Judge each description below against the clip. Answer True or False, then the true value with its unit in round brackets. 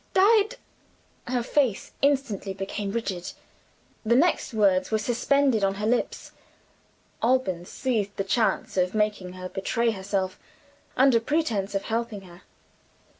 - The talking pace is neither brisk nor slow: False (130 wpm)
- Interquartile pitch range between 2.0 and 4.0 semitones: False (4.5 semitones)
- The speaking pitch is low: False (215 Hz)